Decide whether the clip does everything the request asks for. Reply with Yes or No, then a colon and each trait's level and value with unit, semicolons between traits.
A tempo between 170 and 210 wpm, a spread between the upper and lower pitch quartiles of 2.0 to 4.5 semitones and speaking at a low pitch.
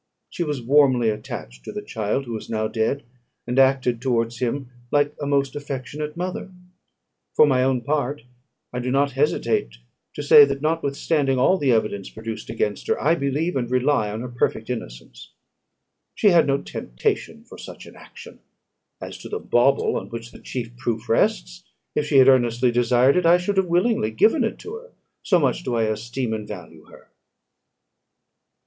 Yes: average, 180 wpm; average, 4.1 semitones; low, 130 Hz